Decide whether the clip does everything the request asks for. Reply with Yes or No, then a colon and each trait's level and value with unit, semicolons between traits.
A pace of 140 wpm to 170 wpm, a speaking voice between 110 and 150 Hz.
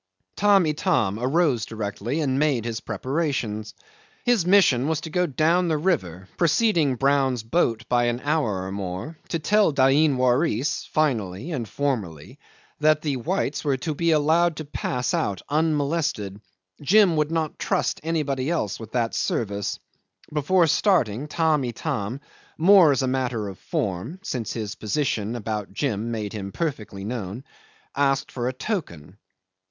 Yes: average, 150 wpm; low, 135 Hz